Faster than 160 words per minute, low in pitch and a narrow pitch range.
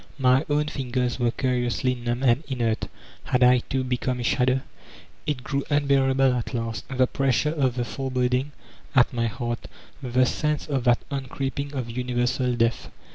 Yes: average, 170 wpm; low, 125 Hz; narrow, 1.7 semitones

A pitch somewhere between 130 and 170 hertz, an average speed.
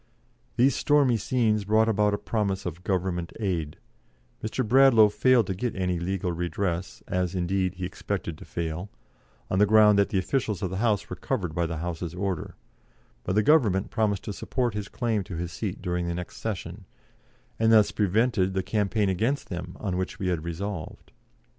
No: very low, 95 Hz; average, 185 wpm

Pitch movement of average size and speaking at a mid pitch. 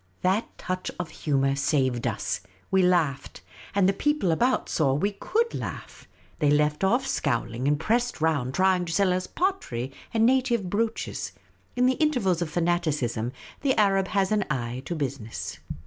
No: wide, 7.2 semitones; medium, 180 Hz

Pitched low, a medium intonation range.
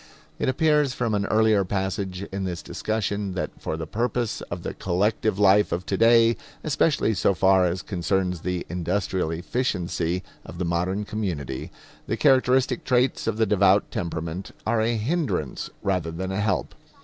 Yes: low, 100 Hz; average, 3.8 semitones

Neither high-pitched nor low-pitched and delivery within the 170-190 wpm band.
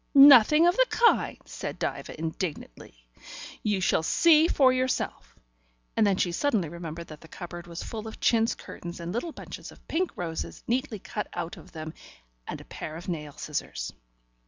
Yes: medium, 180 Hz; average, 175 wpm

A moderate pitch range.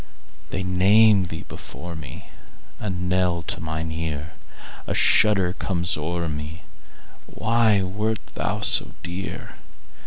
Yes: average, 3.2 semitones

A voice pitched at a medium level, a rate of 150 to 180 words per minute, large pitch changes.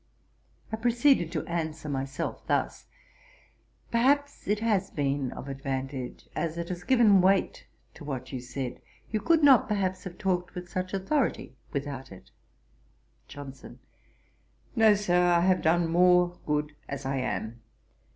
No: medium, 175 Hz; average, 140 wpm; wide, 6.4 semitones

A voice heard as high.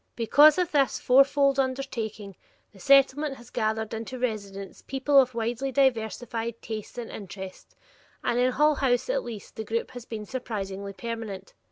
Yes: high, 235 Hz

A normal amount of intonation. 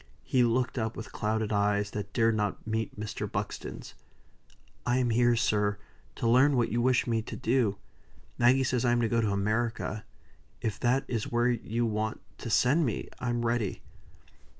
No: narrow, 2.1 semitones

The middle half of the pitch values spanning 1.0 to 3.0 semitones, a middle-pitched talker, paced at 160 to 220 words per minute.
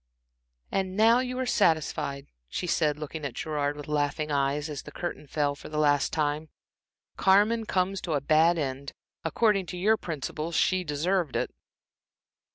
No: average, 4.3 semitones; medium, 155 Hz; average, 165 wpm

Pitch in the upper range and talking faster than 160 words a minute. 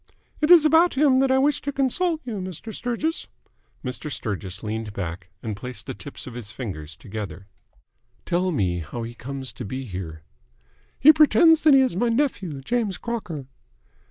No: medium, 150 Hz; average, 175 wpm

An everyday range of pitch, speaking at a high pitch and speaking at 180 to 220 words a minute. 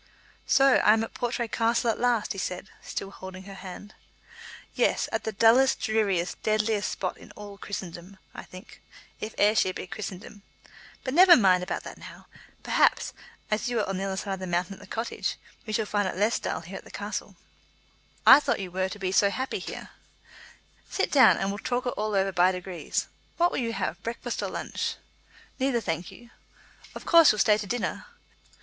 Yes: average, 3.5 semitones; high, 210 Hz; average, 200 wpm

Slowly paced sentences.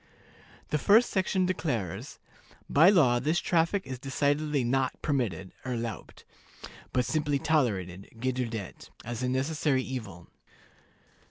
Yes: slow, 110 wpm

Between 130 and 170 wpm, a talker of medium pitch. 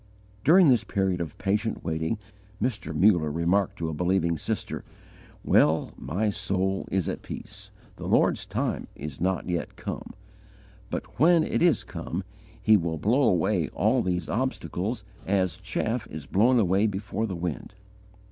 No: average, 150 wpm; very low, 95 Hz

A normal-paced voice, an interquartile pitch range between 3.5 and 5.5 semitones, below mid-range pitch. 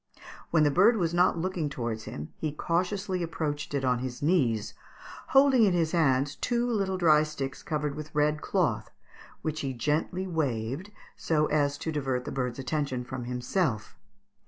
No: average, 165 wpm; average, 4.8 semitones; medium, 150 Hz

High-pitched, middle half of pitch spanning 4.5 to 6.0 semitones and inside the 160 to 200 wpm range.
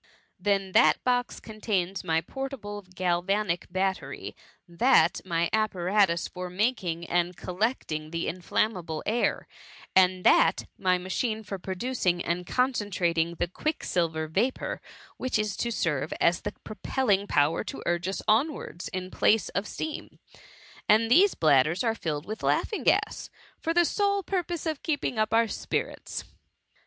No: high, 195 Hz; average, 4.8 semitones; average, 145 wpm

